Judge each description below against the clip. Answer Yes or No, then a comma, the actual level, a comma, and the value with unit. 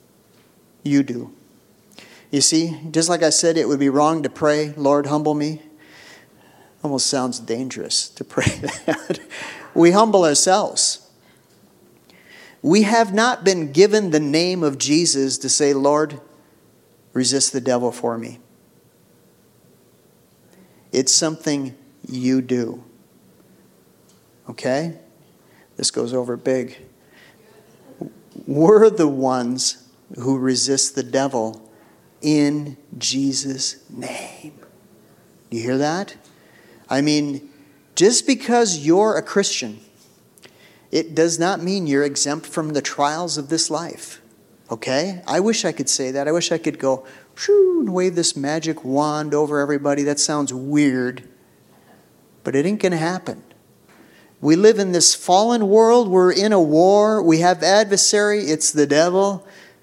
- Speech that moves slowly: Yes, slow, 130 wpm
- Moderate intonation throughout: Yes, average, 4.6 semitones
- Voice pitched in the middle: Yes, medium, 150 Hz